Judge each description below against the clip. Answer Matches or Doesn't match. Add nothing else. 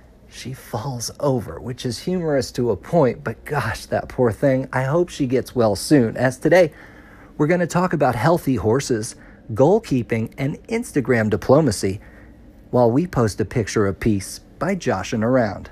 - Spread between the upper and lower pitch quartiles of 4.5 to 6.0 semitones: Matches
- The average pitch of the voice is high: Doesn't match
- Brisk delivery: Doesn't match